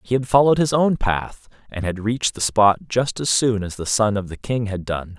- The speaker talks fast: Yes, fast, 255 wpm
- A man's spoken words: Yes, male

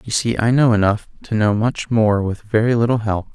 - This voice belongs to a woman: No, male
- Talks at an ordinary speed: No, fast, 235 wpm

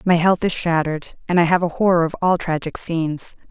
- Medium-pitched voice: Yes, medium, 170 Hz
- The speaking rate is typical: No, fast, 220 wpm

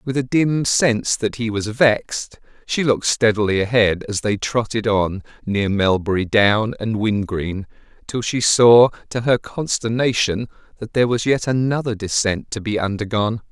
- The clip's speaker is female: No, male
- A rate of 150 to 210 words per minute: Yes, average, 160 wpm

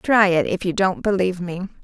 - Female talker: Yes, female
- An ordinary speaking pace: No, fast, 230 wpm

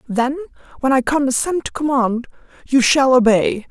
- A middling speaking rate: Yes, average, 145 wpm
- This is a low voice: No, very high, 265 Hz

